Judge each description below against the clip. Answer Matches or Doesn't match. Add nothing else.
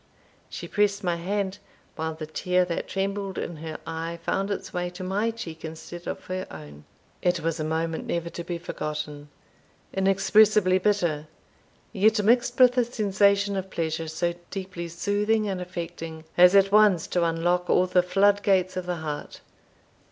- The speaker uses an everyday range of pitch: Matches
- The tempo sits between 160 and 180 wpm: Matches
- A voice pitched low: Doesn't match